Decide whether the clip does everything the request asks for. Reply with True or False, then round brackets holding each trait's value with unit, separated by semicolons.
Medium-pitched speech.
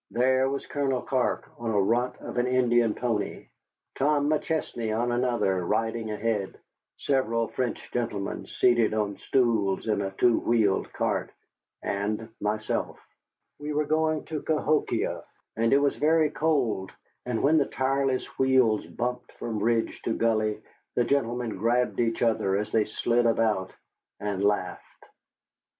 False (120 Hz)